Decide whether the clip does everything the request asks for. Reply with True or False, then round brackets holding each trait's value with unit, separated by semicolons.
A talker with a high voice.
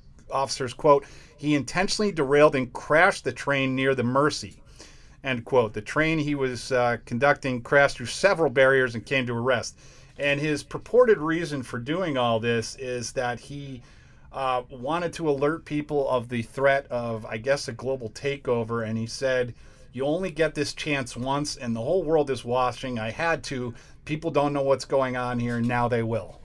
False (135 Hz)